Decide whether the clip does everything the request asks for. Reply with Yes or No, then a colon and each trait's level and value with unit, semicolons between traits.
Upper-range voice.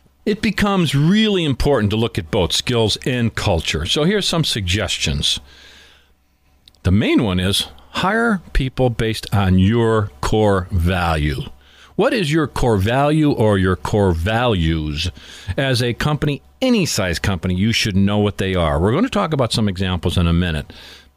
No: low, 105 Hz